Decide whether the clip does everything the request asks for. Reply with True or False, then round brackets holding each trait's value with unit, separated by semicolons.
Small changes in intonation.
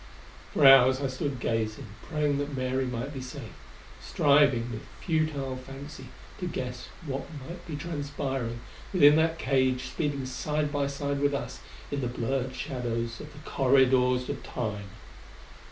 True (2.3 semitones)